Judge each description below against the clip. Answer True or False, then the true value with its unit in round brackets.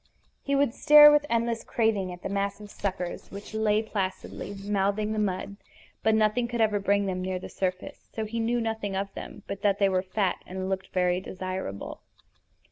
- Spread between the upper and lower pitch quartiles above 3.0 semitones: False (2.7 semitones)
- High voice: True (200 Hz)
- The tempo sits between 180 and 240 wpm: True (190 wpm)